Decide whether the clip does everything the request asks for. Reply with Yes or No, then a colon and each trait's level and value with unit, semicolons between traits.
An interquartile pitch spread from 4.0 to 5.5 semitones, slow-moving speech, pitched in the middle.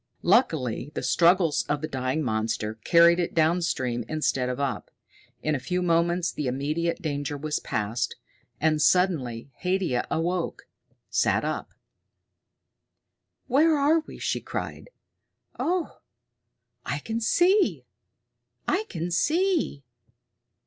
Yes: average, 5.2 semitones; slow, 115 wpm; medium, 165 Hz